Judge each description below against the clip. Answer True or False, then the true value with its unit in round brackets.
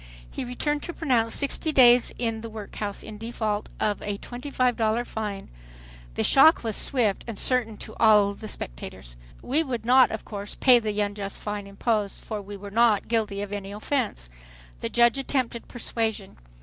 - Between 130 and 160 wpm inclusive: False (175 wpm)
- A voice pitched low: False (220 Hz)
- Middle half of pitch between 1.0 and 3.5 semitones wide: True (3.0 semitones)